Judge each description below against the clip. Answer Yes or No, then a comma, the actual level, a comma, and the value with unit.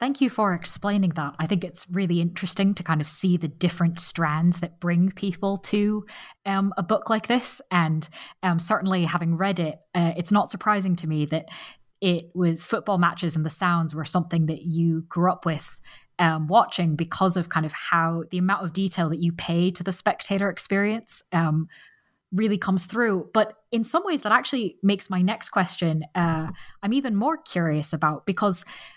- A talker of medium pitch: Yes, medium, 180 Hz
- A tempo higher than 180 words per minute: Yes, average, 190 wpm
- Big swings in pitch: No, average, 3.5 semitones